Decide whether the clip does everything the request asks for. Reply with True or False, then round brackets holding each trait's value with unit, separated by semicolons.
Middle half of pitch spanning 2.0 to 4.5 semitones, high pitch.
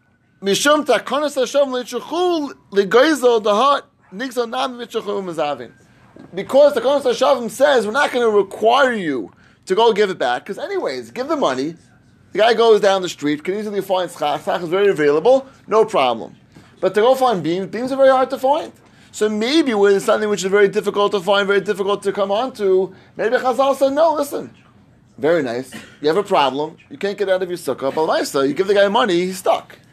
False (5.2 semitones; 210 Hz)